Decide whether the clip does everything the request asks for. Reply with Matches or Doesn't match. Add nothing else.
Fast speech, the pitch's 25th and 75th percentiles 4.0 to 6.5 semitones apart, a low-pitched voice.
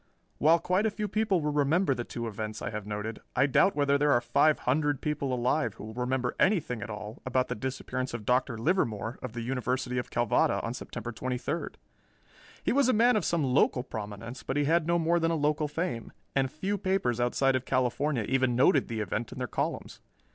Matches